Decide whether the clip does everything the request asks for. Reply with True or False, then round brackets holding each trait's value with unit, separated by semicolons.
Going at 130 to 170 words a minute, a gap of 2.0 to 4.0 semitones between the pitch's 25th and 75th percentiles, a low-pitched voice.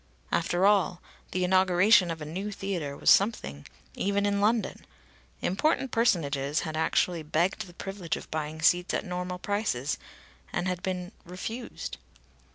False (145 wpm; 3.6 semitones; 180 Hz)